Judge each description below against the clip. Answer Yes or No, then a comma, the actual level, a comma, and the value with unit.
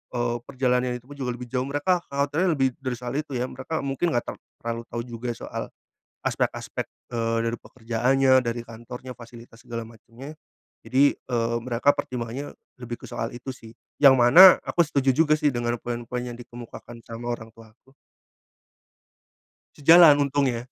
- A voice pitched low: Yes, low, 125 Hz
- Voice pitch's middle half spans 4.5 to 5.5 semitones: No, average, 2.8 semitones